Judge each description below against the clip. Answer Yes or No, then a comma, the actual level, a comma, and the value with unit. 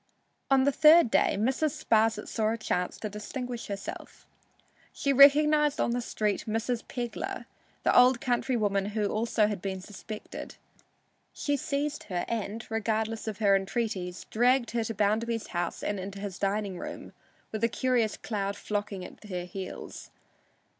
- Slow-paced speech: No, average, 155 wpm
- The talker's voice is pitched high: Yes, high, 220 Hz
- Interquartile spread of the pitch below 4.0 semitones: Yes, average, 3.5 semitones